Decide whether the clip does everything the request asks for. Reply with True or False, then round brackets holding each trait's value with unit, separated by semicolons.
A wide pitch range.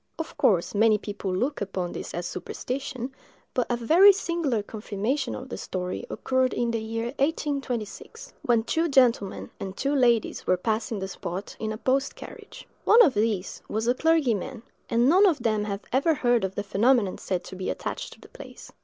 False (4.8 semitones)